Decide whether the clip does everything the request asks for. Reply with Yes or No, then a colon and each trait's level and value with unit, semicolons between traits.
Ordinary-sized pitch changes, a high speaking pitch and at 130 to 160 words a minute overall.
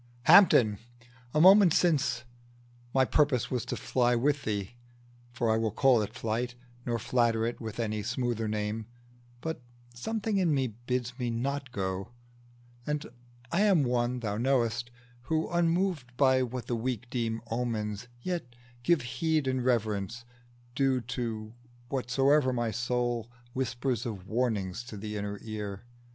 No: average, 3.1 semitones; low, 120 Hz; average, 145 wpm